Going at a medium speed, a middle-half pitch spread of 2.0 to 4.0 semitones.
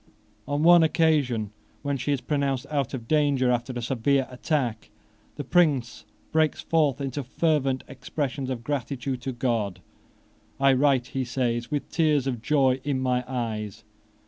Yes: average, 150 wpm; average, 2.9 semitones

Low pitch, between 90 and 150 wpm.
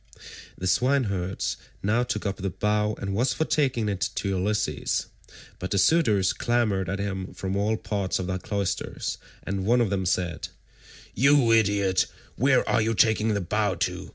No: low, 100 Hz; average, 170 wpm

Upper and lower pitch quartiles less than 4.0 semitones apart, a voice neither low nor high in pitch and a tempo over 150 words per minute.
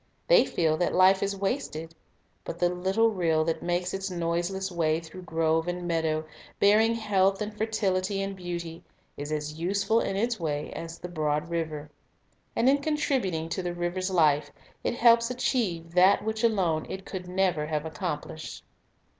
Yes: average, 3.6 semitones; medium, 180 Hz; average, 165 wpm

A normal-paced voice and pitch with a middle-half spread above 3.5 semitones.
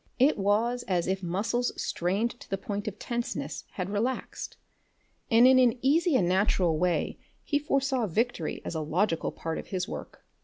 Yes: average, 175 wpm; average, 5.2 semitones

